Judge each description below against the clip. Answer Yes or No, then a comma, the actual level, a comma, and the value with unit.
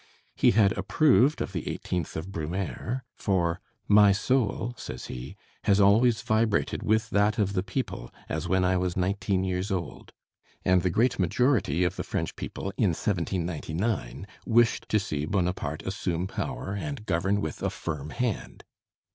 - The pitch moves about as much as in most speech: Yes, average, 3.6 semitones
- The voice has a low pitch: Yes, very low, 95 Hz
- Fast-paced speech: No, average, 155 wpm